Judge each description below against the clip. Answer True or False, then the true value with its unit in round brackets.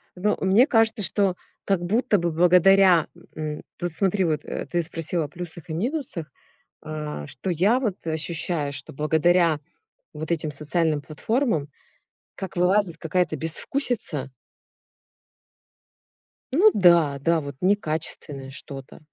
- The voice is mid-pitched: True (170 Hz)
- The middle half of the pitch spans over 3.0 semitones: True (4.0 semitones)